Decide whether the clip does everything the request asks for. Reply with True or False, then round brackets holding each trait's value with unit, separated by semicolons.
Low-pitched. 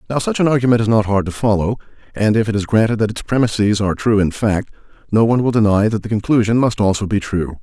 True (110 Hz)